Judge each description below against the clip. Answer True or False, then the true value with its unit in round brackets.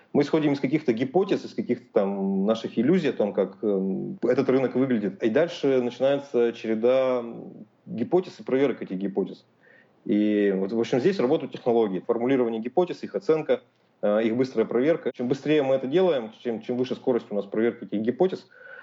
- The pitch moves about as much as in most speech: True (3.8 semitones)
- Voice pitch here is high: False (125 Hz)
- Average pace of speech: False (170 wpm)